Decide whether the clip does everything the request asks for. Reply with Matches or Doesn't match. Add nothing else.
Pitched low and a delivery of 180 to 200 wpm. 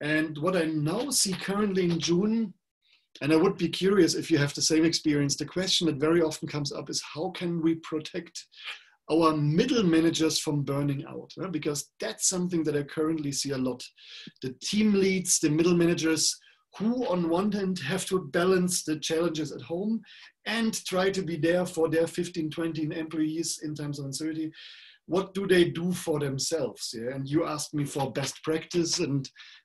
Doesn't match